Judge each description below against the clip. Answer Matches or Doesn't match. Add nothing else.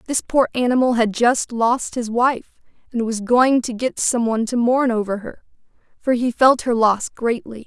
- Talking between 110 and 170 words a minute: Doesn't match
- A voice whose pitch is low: Doesn't match